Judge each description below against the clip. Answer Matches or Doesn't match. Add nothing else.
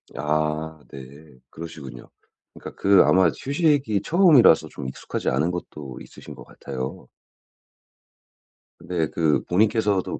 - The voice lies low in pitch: Matches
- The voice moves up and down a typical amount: Doesn't match